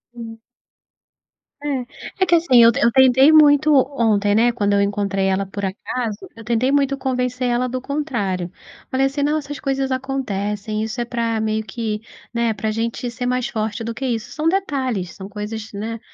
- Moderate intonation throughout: Yes, average, 3.9 semitones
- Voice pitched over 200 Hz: Yes, high, 235 Hz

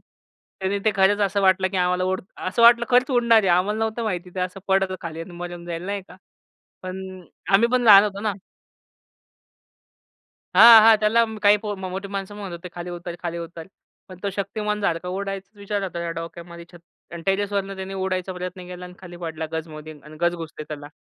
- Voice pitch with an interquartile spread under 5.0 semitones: Yes, average, 2.8 semitones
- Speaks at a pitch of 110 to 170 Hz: No, high, 190 Hz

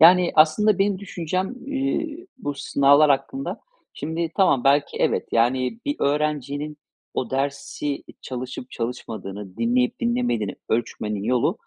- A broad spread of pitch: Yes, wide, 7.9 semitones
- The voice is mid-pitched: Yes, medium, 150 Hz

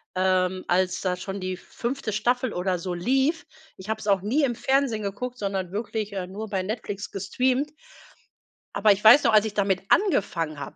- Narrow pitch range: No, average, 4.4 semitones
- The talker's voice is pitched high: Yes, high, 205 Hz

